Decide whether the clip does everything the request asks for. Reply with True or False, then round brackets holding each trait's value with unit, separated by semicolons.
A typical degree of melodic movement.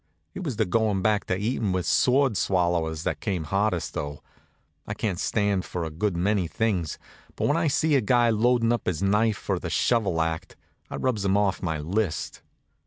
True (4.4 semitones)